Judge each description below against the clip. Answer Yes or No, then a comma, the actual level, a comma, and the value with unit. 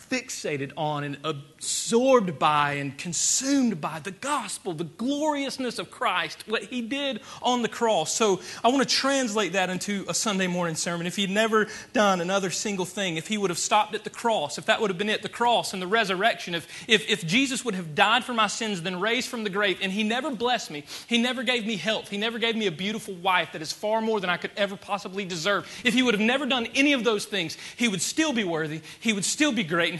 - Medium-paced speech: No, fast, 240 wpm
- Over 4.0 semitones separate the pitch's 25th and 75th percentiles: Yes, average, 4.5 semitones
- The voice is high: Yes, high, 210 Hz